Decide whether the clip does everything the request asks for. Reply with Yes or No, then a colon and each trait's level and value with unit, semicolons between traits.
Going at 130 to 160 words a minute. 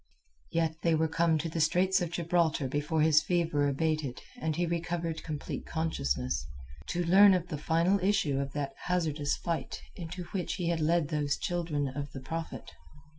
No: average, 175 wpm